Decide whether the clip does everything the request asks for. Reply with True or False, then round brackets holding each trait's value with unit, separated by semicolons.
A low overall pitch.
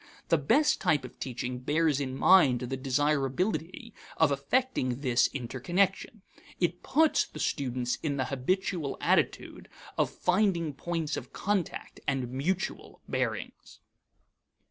False (145 Hz)